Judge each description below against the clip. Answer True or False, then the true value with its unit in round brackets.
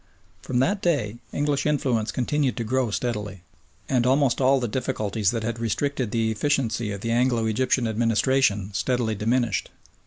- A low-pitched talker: True (120 Hz)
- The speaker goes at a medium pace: True (155 wpm)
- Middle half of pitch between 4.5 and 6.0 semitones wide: False (3.1 semitones)